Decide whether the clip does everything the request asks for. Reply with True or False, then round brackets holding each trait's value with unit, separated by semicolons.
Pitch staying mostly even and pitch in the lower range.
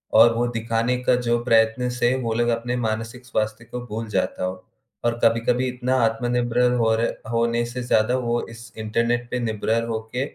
True (1.5 semitones; 115 Hz)